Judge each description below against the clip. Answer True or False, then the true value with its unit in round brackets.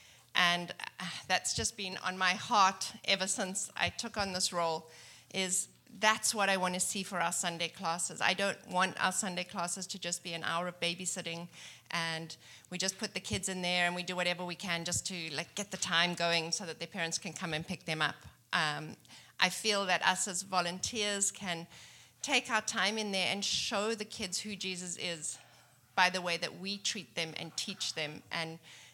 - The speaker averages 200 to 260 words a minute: True (205 wpm)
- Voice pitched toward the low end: False (180 Hz)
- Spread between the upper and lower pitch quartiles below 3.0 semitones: True (2.5 semitones)